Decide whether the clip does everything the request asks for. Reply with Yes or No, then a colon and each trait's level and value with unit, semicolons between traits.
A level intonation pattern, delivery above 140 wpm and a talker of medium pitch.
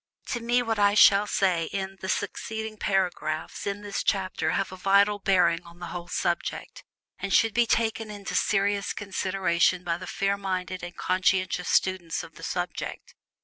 No: narrow, 2.2 semitones; average, 170 wpm; high, 195 Hz